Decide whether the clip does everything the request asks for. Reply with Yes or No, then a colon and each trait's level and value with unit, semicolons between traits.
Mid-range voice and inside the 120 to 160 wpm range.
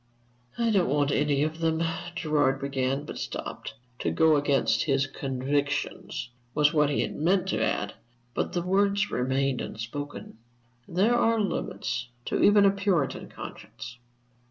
Yes: medium, 145 Hz; average, 145 wpm